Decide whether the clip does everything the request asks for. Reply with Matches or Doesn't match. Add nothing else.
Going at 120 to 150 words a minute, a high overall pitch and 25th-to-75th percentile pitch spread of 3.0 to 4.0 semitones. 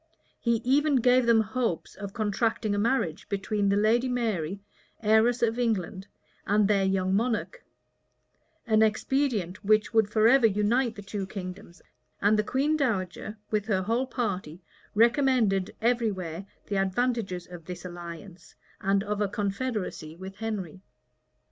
Matches